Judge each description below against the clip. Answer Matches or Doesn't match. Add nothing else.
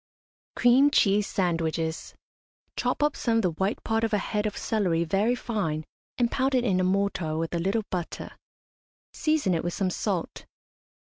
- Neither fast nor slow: Matches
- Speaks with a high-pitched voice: Matches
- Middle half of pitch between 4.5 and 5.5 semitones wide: Matches